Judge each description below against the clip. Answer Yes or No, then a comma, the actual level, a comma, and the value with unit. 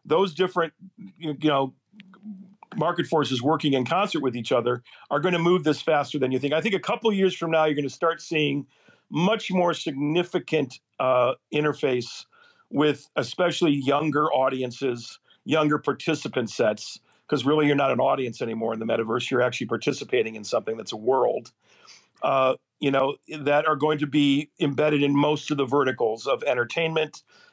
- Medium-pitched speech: Yes, medium, 150 Hz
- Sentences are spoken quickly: No, average, 175 wpm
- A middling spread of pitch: Yes, average, 3.9 semitones